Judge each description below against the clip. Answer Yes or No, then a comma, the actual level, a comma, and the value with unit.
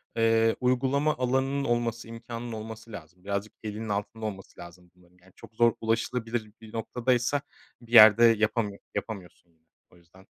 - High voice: No, low, 115 Hz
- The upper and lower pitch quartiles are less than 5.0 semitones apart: Yes, average, 2.9 semitones